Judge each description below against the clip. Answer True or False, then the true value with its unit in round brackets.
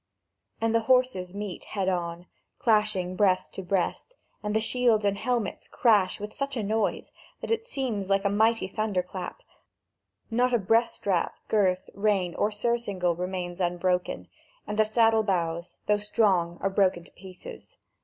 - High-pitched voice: True (200 Hz)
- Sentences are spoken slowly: False (160 wpm)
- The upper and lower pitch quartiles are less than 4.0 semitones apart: True (3.4 semitones)